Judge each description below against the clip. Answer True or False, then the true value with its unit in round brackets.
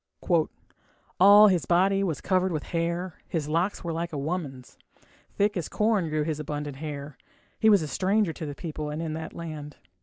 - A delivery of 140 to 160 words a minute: False (185 wpm)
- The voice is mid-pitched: True (165 Hz)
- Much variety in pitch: False (3.6 semitones)